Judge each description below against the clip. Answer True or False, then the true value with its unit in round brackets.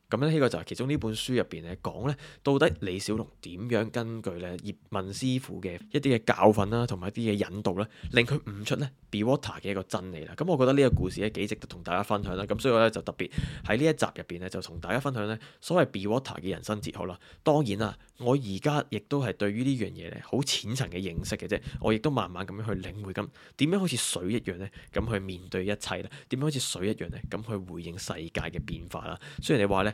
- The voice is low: True (105 Hz)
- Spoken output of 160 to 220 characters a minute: False (380 characters per minute)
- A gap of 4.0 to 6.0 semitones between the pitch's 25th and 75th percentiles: True (4.5 semitones)